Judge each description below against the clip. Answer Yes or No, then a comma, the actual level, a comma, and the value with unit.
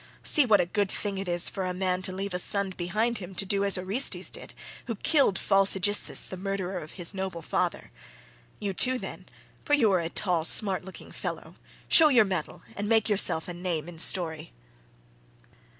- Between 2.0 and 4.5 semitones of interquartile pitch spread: Yes, narrow, 2.4 semitones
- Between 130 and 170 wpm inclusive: No, average, 190 wpm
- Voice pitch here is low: No, high, 190 Hz